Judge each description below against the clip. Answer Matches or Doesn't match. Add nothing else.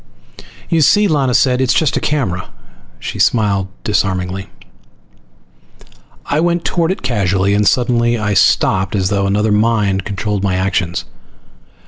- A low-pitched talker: Matches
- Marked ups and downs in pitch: Doesn't match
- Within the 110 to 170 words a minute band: Matches